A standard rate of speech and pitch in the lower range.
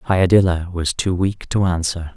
Yes: average, 165 wpm; very low, 90 Hz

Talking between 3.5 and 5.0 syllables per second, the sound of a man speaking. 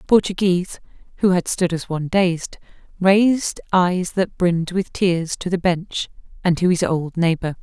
No: 4.6 syllables/s; female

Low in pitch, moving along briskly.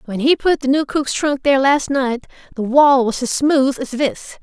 No: very high, 270 Hz; fast, 230 wpm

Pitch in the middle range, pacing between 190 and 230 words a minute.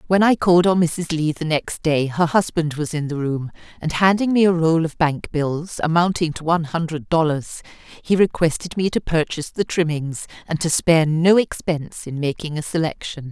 Yes: medium, 160 Hz; average, 200 wpm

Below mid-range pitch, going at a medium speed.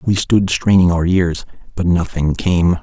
Yes: very low, 90 Hz; average, 170 wpm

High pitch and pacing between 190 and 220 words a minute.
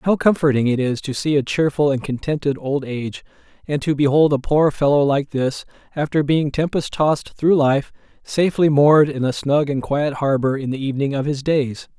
No: medium, 145 Hz; average, 200 wpm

